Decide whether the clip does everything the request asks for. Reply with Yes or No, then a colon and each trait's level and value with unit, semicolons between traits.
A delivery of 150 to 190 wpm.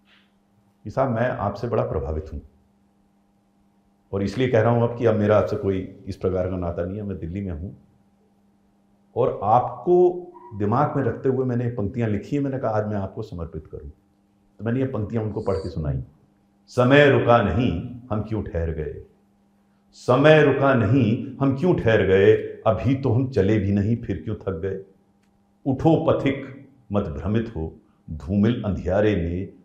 Yes: average, 170 wpm